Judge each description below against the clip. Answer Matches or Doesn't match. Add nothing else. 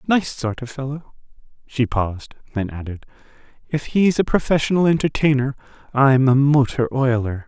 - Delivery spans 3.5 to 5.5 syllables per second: Matches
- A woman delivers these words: Doesn't match